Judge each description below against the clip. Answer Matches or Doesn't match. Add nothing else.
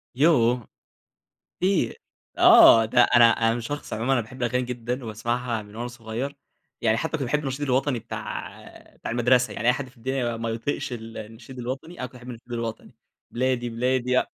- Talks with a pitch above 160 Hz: Doesn't match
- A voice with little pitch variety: Matches